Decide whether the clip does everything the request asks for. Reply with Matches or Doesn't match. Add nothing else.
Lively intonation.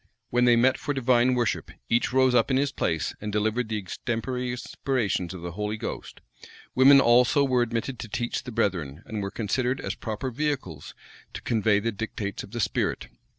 Doesn't match